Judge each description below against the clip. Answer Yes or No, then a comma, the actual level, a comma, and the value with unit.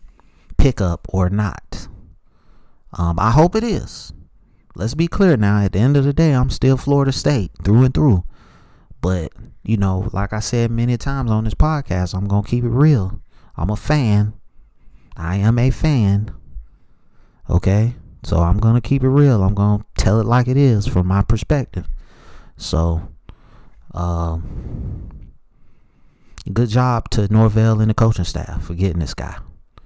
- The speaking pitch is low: Yes, low, 105 Hz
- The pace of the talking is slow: No, average, 165 wpm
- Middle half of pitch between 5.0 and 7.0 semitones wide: Yes, wide, 5.5 semitones